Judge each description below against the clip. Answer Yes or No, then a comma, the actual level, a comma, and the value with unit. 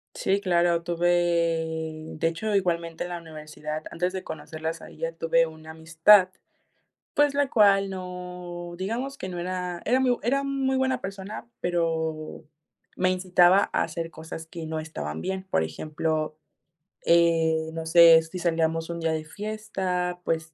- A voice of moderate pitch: Yes, medium, 175 Hz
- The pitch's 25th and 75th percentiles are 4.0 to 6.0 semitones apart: No, average, 2.8 semitones